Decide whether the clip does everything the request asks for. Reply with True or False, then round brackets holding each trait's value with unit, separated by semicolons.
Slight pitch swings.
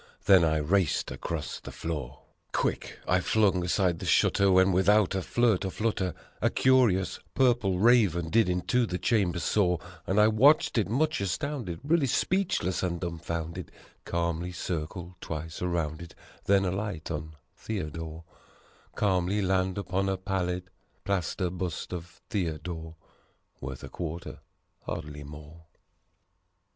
False (3.2 semitones)